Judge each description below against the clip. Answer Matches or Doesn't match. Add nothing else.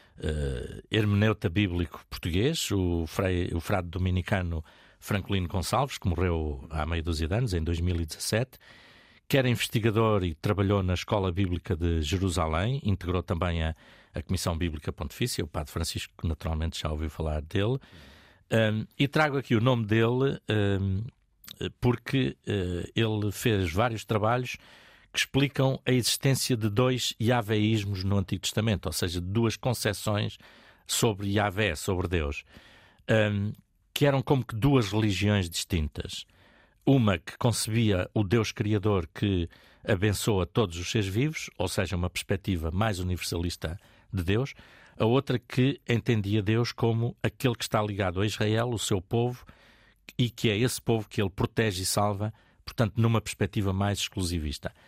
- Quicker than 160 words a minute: Doesn't match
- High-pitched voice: Doesn't match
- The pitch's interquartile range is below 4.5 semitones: Matches